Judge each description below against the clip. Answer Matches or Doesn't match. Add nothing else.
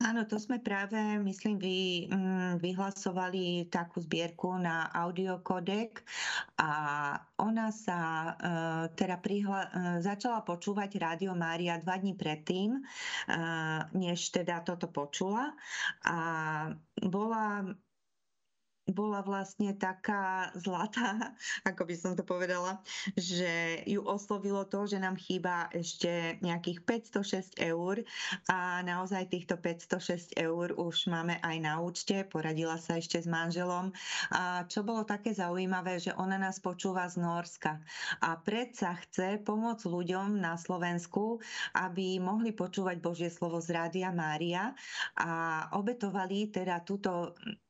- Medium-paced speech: Matches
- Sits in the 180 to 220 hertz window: Matches